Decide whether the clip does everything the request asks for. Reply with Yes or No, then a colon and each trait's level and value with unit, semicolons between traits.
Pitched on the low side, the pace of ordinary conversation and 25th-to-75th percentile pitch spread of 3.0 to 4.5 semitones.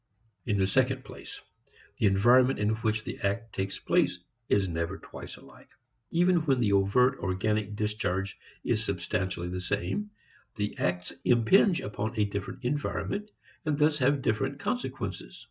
No: low, 110 Hz; average, 145 wpm; average, 5.3 semitones